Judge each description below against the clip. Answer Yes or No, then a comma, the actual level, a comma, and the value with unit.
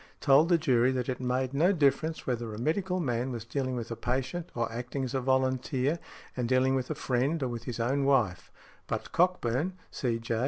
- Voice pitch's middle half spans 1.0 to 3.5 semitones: Yes, average, 2.8 semitones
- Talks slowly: No, average, 200 wpm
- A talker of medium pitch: No, low, 130 Hz